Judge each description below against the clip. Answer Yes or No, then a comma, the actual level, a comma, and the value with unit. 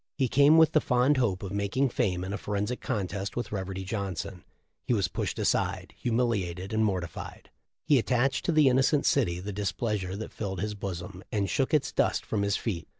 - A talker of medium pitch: No, low, 105 Hz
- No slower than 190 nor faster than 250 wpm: Yes, average, 195 wpm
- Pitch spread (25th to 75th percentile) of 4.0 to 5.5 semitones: Yes, average, 4.7 semitones